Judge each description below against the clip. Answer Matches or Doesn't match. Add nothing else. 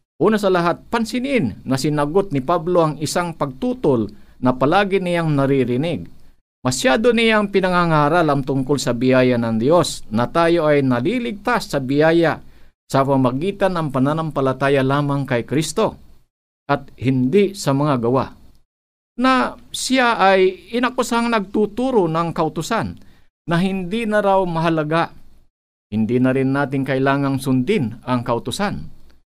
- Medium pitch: Matches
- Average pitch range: Doesn't match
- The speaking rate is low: Doesn't match